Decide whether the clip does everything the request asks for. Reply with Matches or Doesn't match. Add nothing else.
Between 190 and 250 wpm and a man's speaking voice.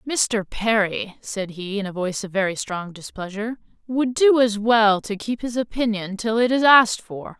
Doesn't match